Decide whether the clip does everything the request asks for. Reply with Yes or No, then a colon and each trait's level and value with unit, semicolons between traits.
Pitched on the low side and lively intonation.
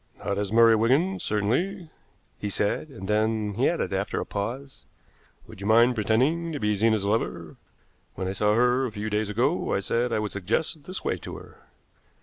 No: low, 110 Hz; average, 3.9 semitones